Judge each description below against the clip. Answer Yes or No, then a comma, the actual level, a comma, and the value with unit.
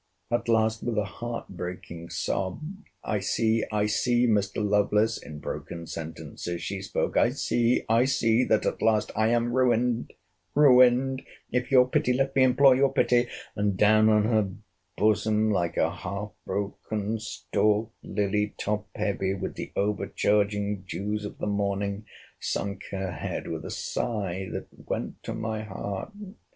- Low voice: Yes, low, 105 Hz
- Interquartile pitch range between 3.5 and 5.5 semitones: No, average, 2.8 semitones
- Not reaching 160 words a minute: Yes, average, 140 wpm